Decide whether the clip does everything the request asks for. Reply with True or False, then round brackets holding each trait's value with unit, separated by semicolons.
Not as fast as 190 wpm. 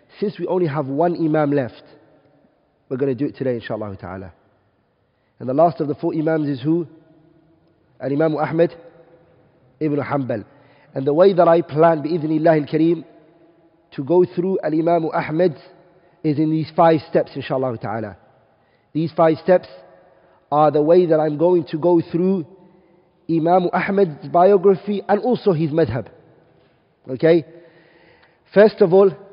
True (145 wpm)